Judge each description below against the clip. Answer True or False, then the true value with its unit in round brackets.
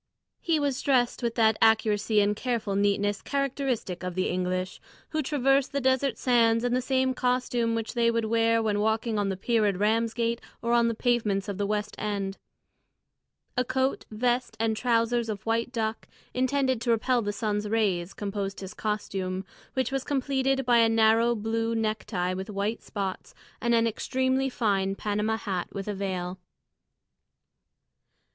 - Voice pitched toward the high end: True (225 Hz)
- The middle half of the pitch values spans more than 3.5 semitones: False (3.1 semitones)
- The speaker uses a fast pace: False (165 wpm)